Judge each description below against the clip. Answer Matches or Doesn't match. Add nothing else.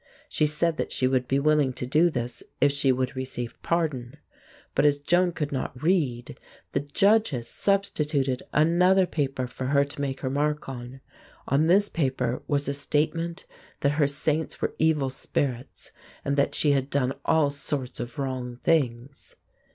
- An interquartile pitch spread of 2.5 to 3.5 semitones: Matches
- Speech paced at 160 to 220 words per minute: Matches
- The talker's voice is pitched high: Doesn't match